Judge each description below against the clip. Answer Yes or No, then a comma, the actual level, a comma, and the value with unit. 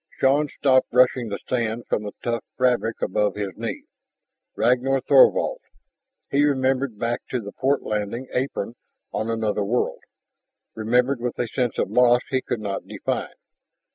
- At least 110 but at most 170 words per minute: Yes, average, 150 wpm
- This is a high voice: No, low, 120 Hz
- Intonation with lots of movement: No, average, 3.0 semitones